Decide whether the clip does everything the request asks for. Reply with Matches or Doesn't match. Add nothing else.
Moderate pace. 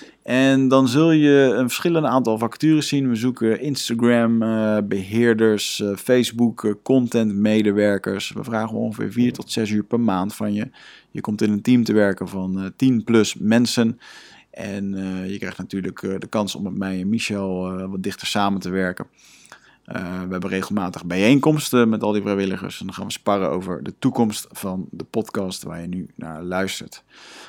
Matches